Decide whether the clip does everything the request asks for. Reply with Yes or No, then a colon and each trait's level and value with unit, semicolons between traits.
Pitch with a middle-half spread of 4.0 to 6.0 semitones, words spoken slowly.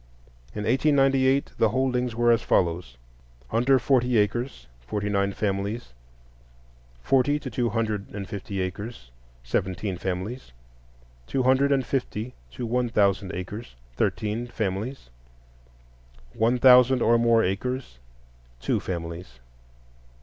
Yes: average, 4.4 semitones; slow, 115 wpm